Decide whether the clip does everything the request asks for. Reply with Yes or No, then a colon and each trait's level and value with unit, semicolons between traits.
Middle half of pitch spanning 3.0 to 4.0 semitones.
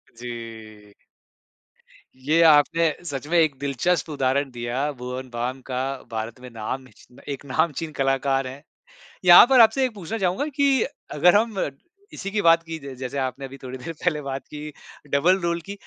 No: average, 4.6 semitones